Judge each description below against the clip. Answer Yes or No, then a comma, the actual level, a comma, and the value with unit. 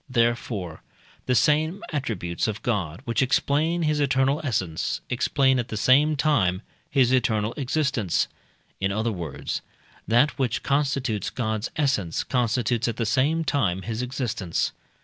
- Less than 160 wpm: Yes, slow, 135 wpm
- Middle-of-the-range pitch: No, low, 125 Hz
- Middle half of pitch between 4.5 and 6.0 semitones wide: Yes, average, 4.8 semitones